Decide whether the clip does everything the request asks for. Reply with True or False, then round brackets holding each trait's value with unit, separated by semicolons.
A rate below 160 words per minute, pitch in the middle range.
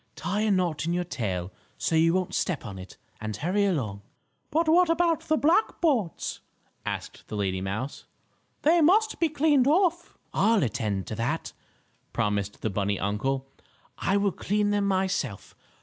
False (165 wpm; 180 Hz)